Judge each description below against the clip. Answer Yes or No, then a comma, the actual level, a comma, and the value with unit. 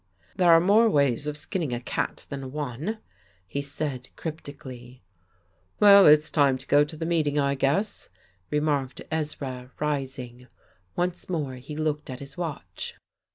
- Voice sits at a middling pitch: Yes, medium, 145 Hz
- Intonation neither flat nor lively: Yes, average, 3.2 semitones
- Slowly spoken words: No, average, 150 wpm